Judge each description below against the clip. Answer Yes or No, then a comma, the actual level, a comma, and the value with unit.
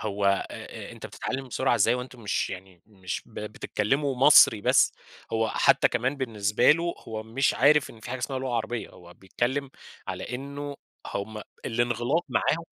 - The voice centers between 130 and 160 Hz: No, low, 120 Hz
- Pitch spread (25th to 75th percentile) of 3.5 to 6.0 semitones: Yes, average, 4.2 semitones